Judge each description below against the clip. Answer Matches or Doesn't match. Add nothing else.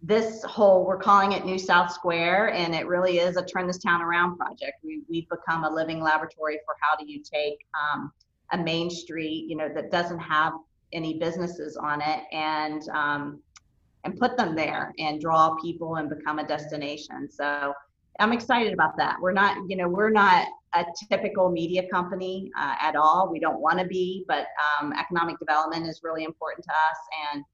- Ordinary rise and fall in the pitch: Matches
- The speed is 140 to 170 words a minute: Doesn't match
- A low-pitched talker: Doesn't match